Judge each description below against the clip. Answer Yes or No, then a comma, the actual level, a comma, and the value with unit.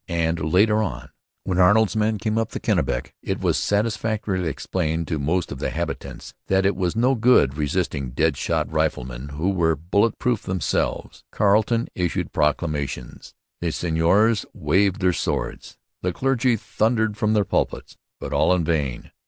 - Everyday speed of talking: Yes, average, 160 wpm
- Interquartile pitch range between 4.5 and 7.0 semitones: Yes, average, 5.1 semitones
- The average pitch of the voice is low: Yes, very low, 95 Hz